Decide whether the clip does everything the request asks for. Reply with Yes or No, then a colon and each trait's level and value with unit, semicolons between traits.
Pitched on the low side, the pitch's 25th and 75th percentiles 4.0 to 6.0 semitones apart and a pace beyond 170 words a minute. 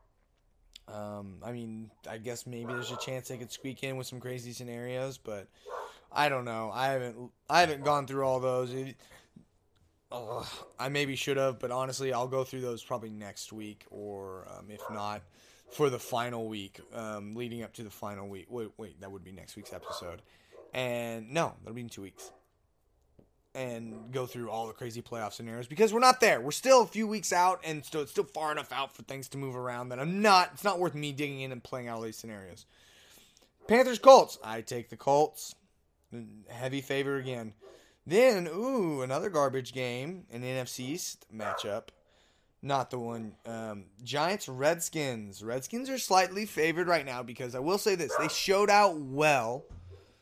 Yes: low, 125 Hz; average, 4.4 semitones; average, 190 wpm